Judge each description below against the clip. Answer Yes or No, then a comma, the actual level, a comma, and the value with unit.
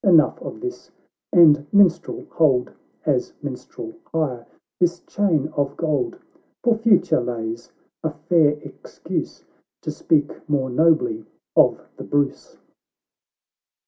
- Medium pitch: Yes, medium, 155 Hz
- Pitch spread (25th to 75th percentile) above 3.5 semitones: Yes, average, 4.2 semitones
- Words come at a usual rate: No, slow, 120 wpm